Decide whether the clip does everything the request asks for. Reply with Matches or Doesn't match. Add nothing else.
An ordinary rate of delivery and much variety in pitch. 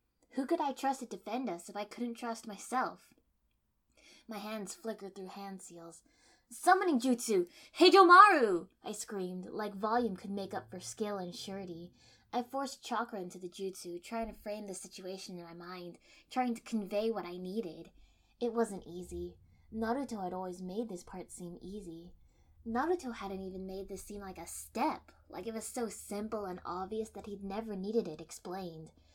Doesn't match